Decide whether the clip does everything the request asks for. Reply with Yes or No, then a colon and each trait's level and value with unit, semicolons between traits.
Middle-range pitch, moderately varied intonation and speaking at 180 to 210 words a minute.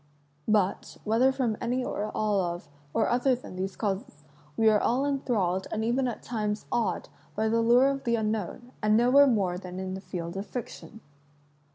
No: high, 220 Hz; average, 4.0 semitones; average, 185 wpm